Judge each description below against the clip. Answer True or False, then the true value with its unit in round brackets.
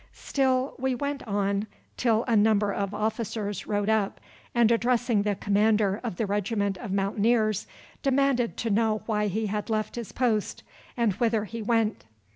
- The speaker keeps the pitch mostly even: True (2.3 semitones)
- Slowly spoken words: False (160 wpm)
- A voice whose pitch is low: False (220 Hz)